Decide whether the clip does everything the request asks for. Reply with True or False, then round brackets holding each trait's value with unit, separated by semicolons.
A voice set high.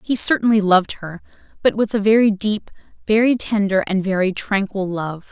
True (205 Hz)